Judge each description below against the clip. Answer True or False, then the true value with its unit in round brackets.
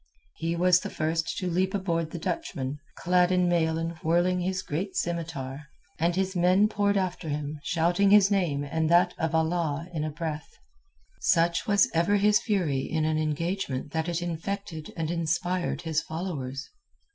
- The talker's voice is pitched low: False (170 Hz)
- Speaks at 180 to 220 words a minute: False (170 wpm)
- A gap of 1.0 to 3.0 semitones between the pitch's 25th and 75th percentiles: True (2.6 semitones)